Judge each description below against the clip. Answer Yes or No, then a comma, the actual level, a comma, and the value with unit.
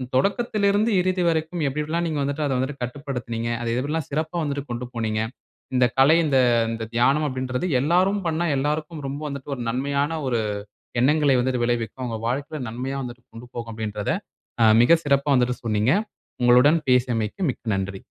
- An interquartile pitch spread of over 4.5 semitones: No, average, 4.2 semitones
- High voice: No, low, 135 Hz